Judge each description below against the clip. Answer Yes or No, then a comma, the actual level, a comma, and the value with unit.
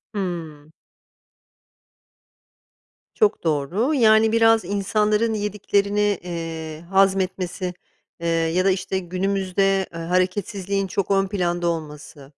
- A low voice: No, high, 190 Hz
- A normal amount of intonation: Yes, average, 3.1 semitones